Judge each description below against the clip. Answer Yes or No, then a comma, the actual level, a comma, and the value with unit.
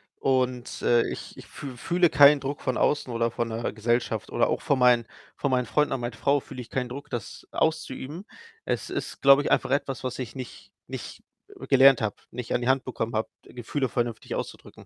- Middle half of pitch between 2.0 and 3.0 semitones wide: Yes, narrow, 2.6 semitones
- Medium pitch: No, low, 125 Hz